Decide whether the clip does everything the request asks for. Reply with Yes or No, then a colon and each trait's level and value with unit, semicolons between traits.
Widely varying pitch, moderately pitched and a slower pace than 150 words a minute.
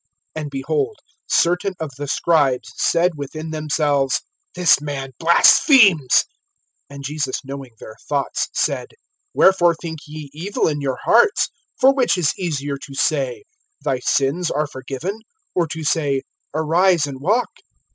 No: average, 4.0 semitones; medium, 155 Hz; slow, 135 wpm